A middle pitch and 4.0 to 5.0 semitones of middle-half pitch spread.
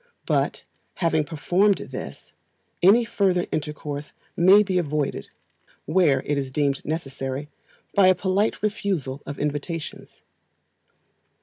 Yes: medium, 160 Hz; average, 4.7 semitones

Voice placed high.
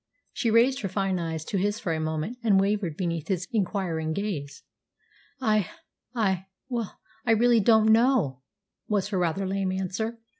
Yes: high, 195 Hz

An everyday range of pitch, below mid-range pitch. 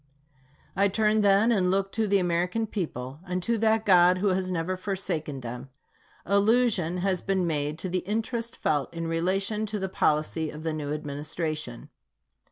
No: average, 4.2 semitones; medium, 185 Hz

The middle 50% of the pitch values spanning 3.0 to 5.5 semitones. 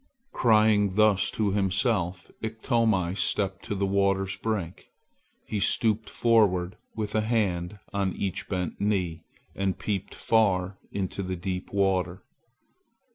No: narrow, 2.6 semitones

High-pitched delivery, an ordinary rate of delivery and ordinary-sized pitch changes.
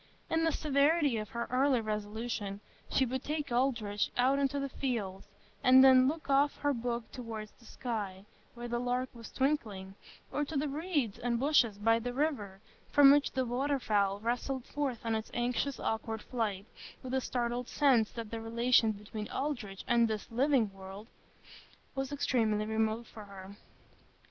Yes: high, 240 Hz; average, 165 wpm; average, 4.0 semitones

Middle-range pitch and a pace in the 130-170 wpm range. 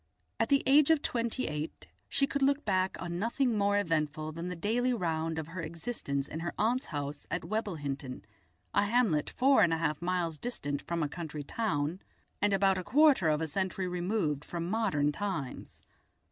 No: medium, 180 Hz; average, 185 wpm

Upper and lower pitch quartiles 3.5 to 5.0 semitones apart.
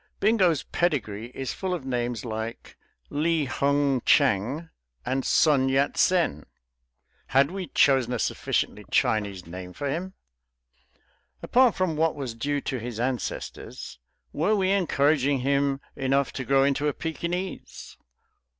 Yes: average, 4.6 semitones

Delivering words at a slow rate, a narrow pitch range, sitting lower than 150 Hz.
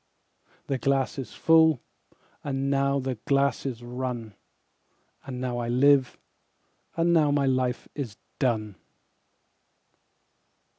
Yes: slow, 105 wpm; narrow, 2.1 semitones; low, 135 Hz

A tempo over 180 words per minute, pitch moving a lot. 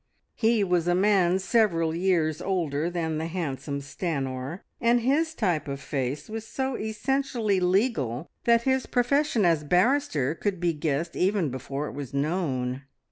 No: average, 150 wpm; wide, 6.7 semitones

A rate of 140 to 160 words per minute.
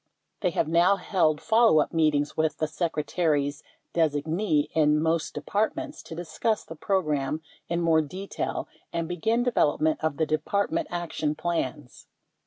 Yes: average, 145 wpm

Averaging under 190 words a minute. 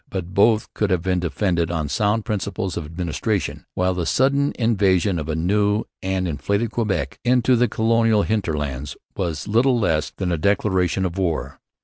Yes: average, 165 wpm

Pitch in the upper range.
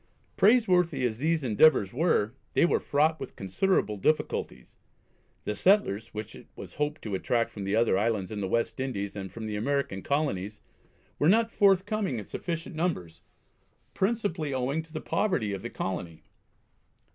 No: low, 130 Hz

